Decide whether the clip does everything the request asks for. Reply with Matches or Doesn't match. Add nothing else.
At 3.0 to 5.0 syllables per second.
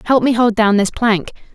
Doesn't match